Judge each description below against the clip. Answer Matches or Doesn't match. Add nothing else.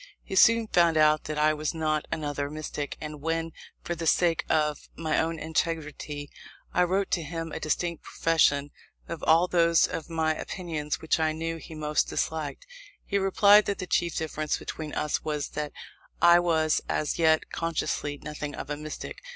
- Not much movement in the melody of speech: Matches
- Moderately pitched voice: Matches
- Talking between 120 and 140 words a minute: Doesn't match